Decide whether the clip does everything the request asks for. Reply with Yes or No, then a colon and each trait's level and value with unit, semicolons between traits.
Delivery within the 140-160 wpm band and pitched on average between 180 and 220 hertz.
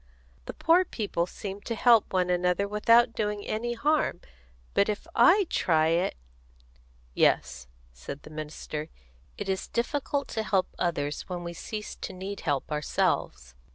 Yes: average, 155 wpm; high, 190 Hz